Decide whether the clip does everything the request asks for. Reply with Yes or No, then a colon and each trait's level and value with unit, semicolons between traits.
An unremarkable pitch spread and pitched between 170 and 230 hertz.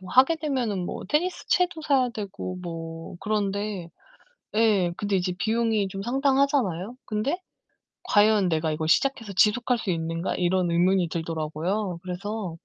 Yes: average, 4.9 semitones; high, 200 Hz